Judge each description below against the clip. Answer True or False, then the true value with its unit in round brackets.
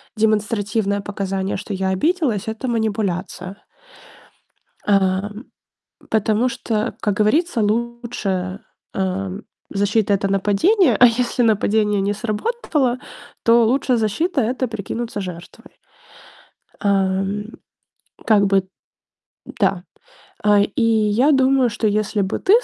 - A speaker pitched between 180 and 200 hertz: False (215 Hz)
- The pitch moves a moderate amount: True (3.2 semitones)